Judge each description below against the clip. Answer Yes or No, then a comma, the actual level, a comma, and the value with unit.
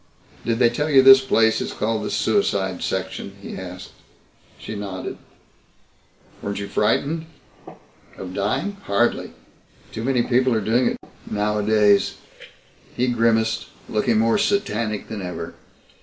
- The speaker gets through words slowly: Yes, slow, 130 wpm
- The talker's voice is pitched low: Yes, low, 110 Hz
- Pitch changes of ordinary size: Yes, average, 3.4 semitones